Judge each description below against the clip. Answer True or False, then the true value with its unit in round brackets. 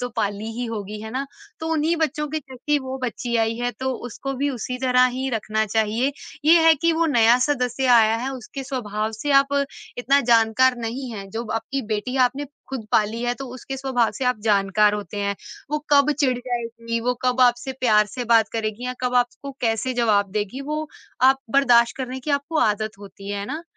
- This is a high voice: True (245 Hz)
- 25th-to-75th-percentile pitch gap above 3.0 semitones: True (3.4 semitones)